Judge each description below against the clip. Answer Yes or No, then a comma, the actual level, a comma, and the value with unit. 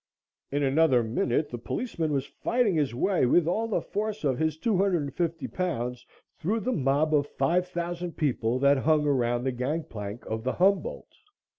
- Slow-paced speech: No, average, 170 wpm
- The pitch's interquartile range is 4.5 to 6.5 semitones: Yes, wide, 5.6 semitones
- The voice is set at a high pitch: No, medium, 150 Hz